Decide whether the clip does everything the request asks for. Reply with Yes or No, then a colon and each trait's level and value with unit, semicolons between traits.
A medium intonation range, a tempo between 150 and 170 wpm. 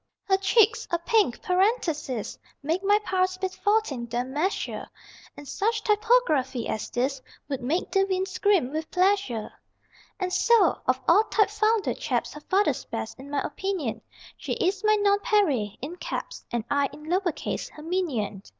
No: wide, 6.5 semitones; average, 160 wpm